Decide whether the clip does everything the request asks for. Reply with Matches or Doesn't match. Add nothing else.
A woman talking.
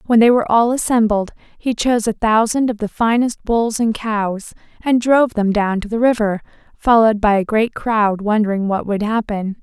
Matches